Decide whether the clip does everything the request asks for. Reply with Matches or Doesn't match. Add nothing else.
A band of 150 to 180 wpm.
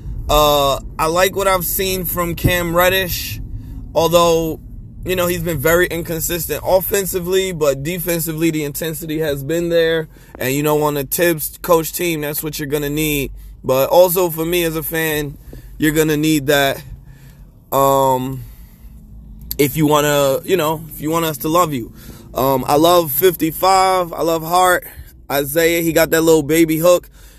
Matches